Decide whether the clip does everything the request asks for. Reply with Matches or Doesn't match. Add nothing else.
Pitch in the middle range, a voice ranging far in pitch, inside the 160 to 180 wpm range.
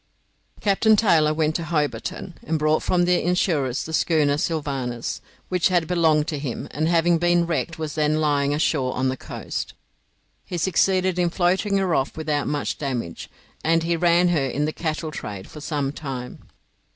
Doesn't match